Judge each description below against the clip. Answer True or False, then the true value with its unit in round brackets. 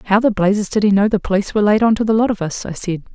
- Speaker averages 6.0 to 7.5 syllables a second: True (7.3 syllables/s)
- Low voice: False (205 Hz)